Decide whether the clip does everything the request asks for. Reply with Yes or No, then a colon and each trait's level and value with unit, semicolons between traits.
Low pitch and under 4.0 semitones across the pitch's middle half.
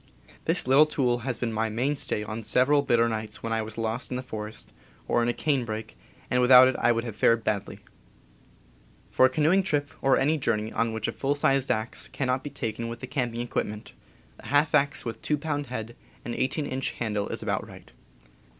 Yes: low, 120 Hz; average, 3.5 semitones